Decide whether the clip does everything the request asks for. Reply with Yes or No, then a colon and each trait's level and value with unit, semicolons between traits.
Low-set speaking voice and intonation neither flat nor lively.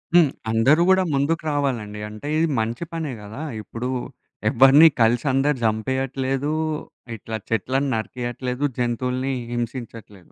Yes: low, 130 Hz; average, 3.7 semitones